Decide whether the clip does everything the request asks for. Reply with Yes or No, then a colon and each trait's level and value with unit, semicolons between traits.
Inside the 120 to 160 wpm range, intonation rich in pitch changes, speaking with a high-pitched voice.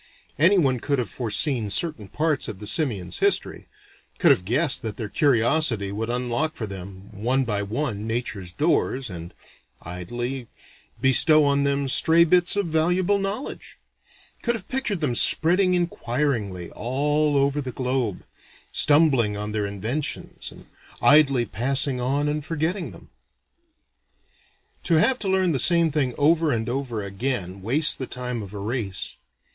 No: average, 150 wpm; wide, 6.2 semitones; low, 130 Hz